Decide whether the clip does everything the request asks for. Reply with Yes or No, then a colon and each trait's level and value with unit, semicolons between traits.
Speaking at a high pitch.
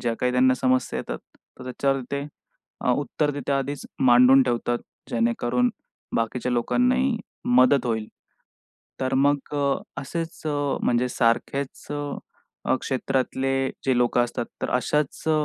No: low, 130 Hz